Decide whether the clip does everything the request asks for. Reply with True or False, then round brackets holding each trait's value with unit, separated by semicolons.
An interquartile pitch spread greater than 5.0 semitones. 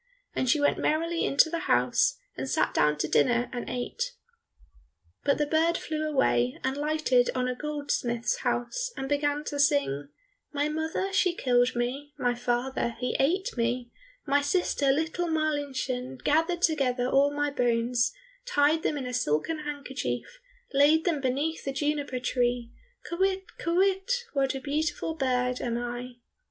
False (4.0 semitones)